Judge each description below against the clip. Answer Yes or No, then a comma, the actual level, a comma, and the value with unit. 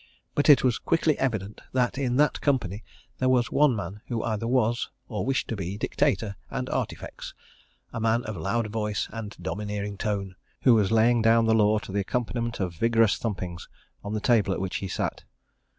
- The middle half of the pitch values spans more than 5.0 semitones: No, average, 3.0 semitones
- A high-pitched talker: No, low, 110 Hz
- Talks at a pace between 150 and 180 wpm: No, average, 190 wpm